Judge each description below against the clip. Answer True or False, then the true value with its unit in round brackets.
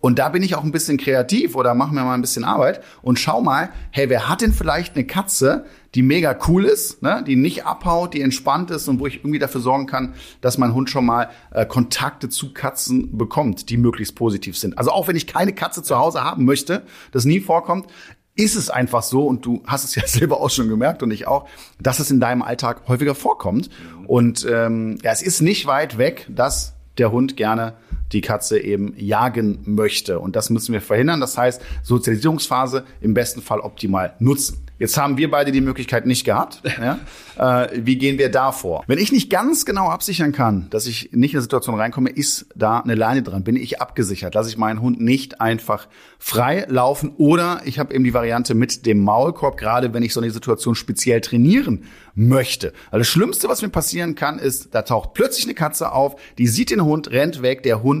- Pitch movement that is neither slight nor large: True (3.9 semitones)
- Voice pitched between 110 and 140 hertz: True (130 Hz)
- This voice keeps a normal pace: False (215 wpm)